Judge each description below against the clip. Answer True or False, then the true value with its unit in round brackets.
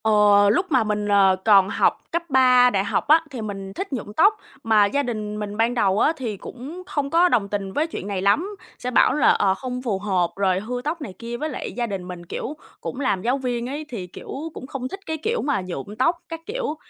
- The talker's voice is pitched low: False (235 Hz)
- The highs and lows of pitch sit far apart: True (5.8 semitones)